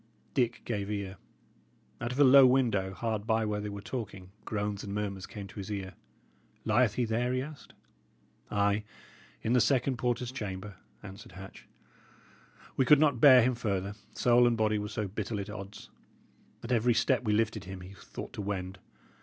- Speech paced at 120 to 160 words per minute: No, average, 180 wpm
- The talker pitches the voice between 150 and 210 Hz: No, low, 105 Hz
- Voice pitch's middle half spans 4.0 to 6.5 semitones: No, average, 3.4 semitones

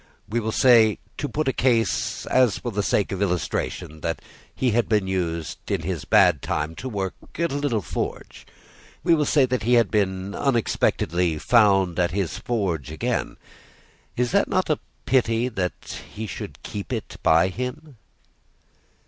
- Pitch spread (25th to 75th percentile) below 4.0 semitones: No, average, 5.2 semitones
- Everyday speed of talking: Yes, average, 165 wpm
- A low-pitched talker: Yes, low, 110 Hz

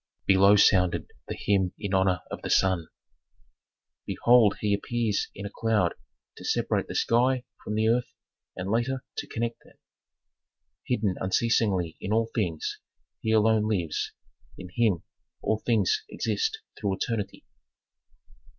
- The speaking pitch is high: No, low, 105 Hz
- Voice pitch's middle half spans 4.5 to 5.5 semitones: No, average, 3.3 semitones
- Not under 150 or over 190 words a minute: No, slow, 135 wpm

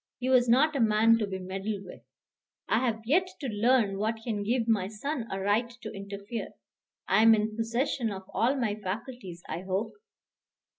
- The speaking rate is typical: Yes, average, 185 wpm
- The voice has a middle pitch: No, high, 220 Hz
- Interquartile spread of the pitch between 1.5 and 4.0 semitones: Yes, average, 3.3 semitones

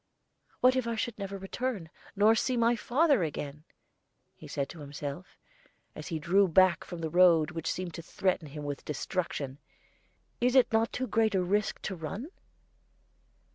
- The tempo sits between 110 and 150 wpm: No, average, 170 wpm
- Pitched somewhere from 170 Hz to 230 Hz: Yes, medium, 185 Hz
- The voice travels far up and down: Yes, wide, 6.1 semitones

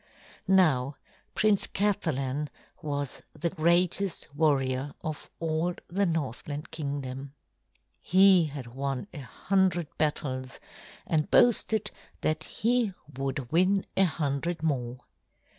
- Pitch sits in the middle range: Yes, medium, 155 Hz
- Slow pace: Yes, slow, 105 wpm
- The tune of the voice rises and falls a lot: No, average, 4.7 semitones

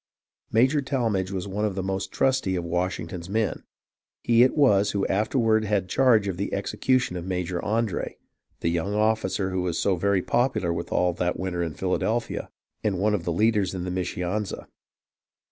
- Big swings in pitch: No, average, 3.4 semitones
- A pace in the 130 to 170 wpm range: No, average, 180 wpm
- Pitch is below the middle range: Yes, very low, 95 Hz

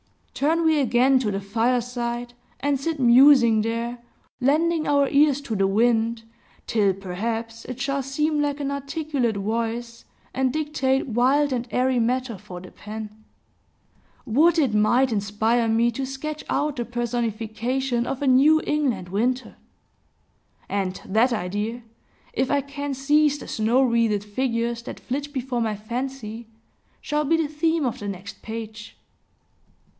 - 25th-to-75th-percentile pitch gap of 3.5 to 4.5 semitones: Yes, average, 3.8 semitones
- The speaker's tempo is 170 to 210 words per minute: No, average, 145 wpm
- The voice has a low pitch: No, high, 245 Hz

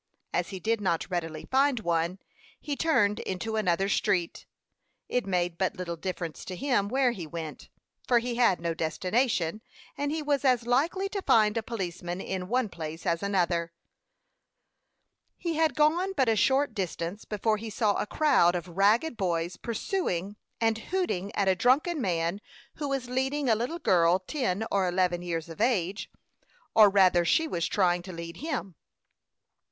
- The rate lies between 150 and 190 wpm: Yes, average, 170 wpm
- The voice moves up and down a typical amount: No, wide, 6.2 semitones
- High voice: Yes, high, 200 Hz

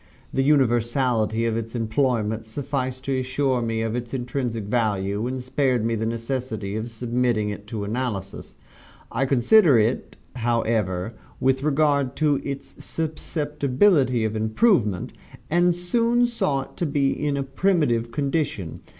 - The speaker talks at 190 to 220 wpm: No, average, 140 wpm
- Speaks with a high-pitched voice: No, low, 125 Hz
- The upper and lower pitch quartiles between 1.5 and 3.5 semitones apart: No, average, 4.0 semitones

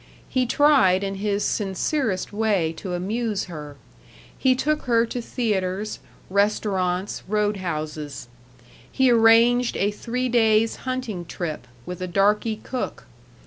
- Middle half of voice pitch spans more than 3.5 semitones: Yes, average, 4.3 semitones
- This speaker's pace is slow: Yes, slow, 125 wpm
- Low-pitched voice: No, high, 210 Hz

